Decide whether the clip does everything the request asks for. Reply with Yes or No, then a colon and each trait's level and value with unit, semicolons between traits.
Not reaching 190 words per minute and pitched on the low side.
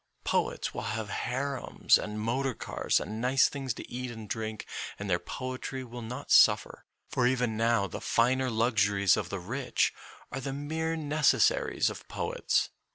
Yes: average, 170 wpm; low, 125 Hz